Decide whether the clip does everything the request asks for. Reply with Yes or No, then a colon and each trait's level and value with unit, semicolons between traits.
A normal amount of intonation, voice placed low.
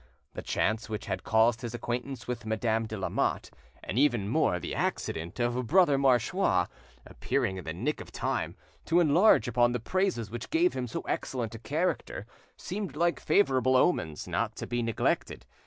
Yes: average, 4.4 semitones; low, 120 Hz